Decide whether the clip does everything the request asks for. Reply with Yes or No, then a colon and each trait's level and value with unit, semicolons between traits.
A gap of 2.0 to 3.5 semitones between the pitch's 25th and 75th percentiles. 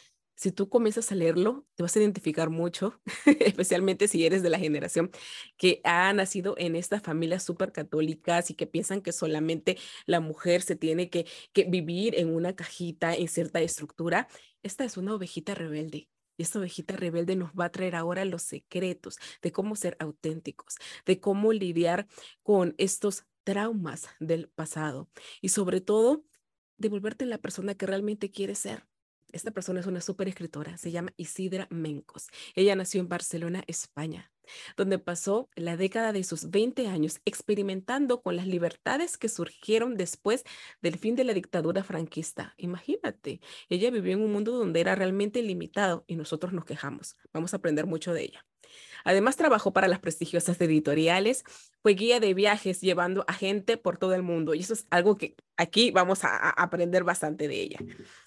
Yes: average, 3.2 semitones